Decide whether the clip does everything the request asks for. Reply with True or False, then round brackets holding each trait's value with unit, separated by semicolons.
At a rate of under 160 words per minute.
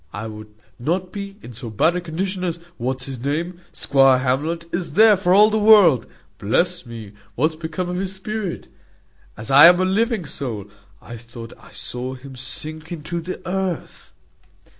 False (175 wpm)